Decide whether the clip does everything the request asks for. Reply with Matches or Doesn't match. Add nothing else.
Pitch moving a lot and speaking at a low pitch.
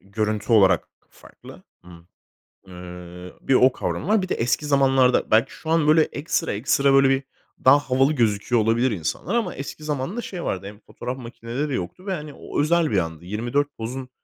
Matches